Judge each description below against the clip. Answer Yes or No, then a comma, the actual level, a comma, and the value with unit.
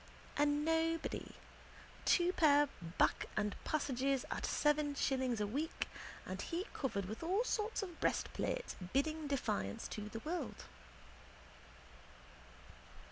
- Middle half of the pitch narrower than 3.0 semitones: No, average, 4.8 semitones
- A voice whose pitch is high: Yes, very high, 290 Hz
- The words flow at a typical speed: No, slow, 115 wpm